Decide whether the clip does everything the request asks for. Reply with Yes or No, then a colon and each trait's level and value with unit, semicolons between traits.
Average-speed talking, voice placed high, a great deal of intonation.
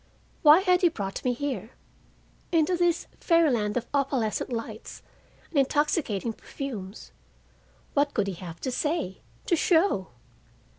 No: slow, 120 wpm; very high, 270 Hz; wide, 7.2 semitones